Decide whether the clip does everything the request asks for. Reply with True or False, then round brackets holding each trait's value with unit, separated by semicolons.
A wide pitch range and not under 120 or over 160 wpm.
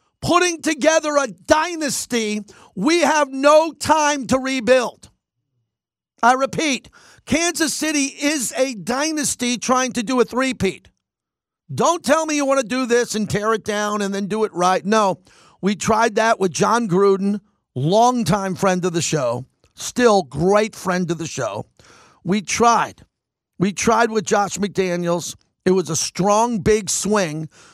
True (5.9 semitones; 150 wpm)